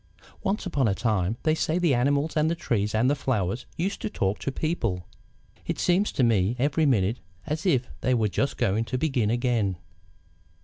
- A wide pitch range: Yes, wide, 6.0 semitones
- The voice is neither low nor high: No, low, 125 Hz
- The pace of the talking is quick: No, average, 190 wpm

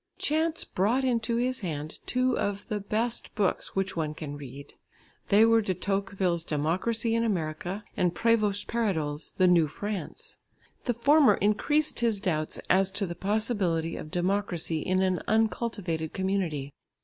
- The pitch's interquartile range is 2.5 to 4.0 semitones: No, average, 5.1 semitones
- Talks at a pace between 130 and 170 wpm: Yes, average, 150 wpm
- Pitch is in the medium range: No, high, 195 Hz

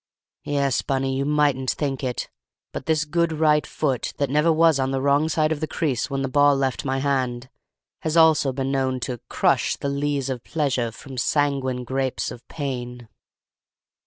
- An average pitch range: No, narrow, 2.2 semitones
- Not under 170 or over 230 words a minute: Yes, average, 180 wpm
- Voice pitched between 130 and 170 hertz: Yes, medium, 140 Hz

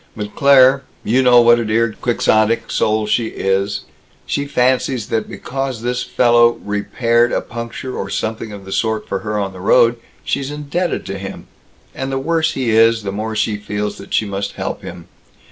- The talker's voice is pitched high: No, low, 115 Hz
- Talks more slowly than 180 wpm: No, average, 185 wpm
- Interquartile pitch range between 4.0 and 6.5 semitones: No, average, 3.3 semitones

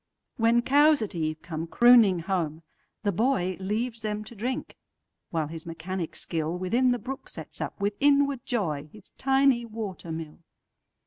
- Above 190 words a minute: No, average, 140 wpm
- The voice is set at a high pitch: Yes, high, 205 Hz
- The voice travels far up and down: Yes, wide, 6.4 semitones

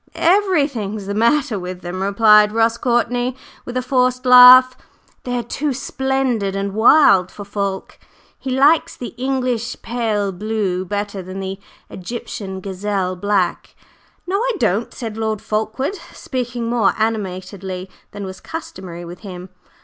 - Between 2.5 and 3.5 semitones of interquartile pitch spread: No, average, 4.5 semitones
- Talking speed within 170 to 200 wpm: No, average, 140 wpm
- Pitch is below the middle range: No, high, 220 Hz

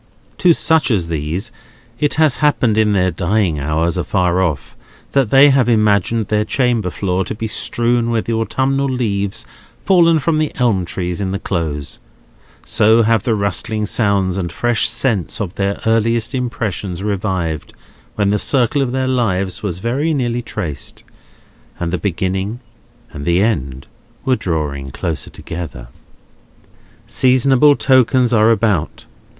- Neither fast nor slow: Yes, average, 145 wpm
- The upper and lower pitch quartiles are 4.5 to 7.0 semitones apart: Yes, average, 5.2 semitones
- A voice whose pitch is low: Yes, low, 105 Hz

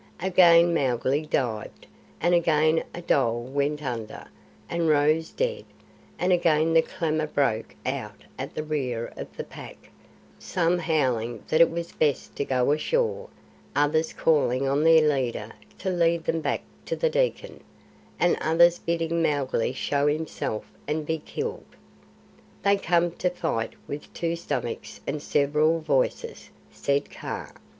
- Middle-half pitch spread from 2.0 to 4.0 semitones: Yes, average, 3.4 semitones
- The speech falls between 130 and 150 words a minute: Yes, average, 145 wpm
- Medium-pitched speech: Yes, medium, 155 Hz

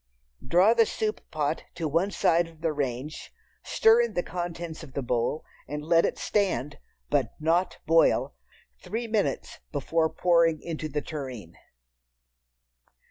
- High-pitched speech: No, medium, 165 Hz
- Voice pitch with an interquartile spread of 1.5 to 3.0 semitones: No, average, 3.5 semitones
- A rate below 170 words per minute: Yes, slow, 135 wpm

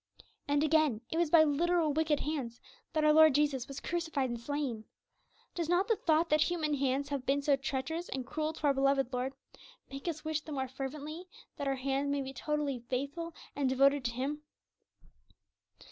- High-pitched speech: Yes, very high, 285 Hz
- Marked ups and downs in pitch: No, narrow, 2.6 semitones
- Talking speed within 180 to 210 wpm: Yes, average, 190 wpm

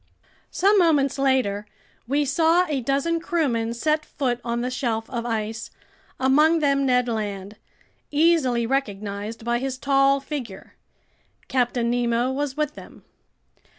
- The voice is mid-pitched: No, very high, 260 Hz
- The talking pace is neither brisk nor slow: No, slow, 130 wpm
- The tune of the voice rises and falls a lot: No, average, 3.8 semitones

